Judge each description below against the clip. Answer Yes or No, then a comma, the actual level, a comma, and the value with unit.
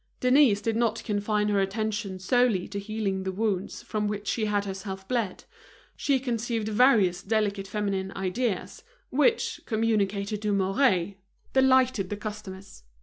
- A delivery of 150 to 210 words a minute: No, average, 140 wpm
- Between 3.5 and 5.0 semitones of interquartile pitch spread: No, average, 2.7 semitones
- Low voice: No, high, 210 Hz